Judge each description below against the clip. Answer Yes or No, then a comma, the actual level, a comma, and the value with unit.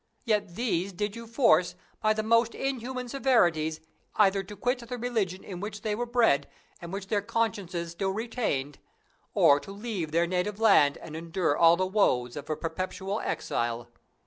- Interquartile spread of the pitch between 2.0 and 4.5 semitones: No, average, 5.3 semitones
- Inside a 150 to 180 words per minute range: Yes, average, 170 wpm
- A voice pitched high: Yes, high, 195 Hz